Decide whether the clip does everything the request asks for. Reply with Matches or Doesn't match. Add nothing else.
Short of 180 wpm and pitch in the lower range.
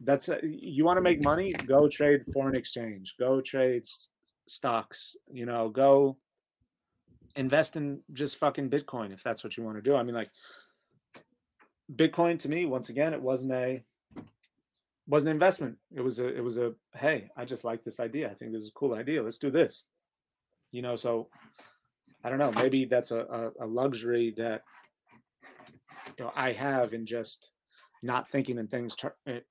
Doesn't match